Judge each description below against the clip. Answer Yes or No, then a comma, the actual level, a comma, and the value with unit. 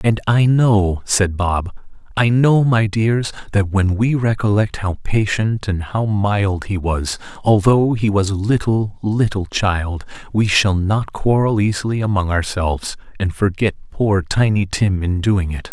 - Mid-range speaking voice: No, low, 100 Hz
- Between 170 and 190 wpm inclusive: No, average, 160 wpm